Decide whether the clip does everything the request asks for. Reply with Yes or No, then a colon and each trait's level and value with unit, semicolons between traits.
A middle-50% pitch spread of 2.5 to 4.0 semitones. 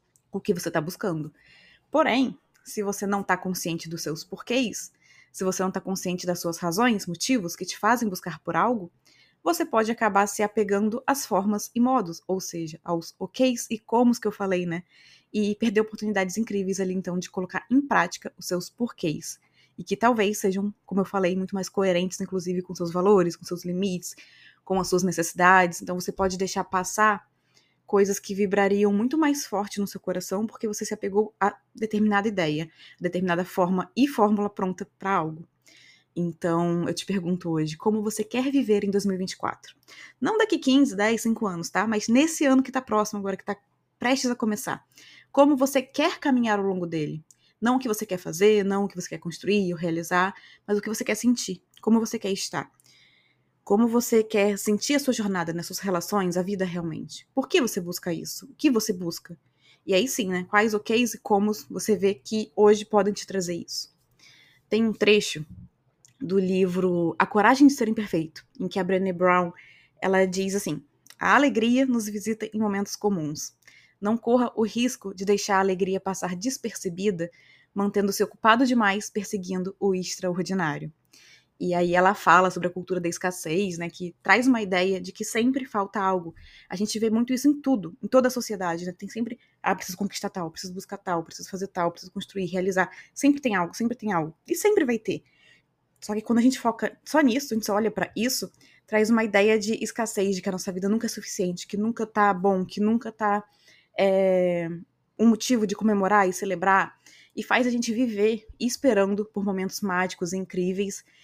Yes: average, 3.3 semitones